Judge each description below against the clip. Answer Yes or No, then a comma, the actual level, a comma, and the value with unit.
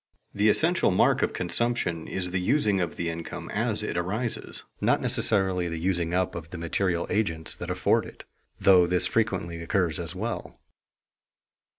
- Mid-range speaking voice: No, very low, 90 Hz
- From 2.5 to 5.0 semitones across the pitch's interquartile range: Yes, average, 3.2 semitones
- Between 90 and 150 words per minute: No, average, 165 wpm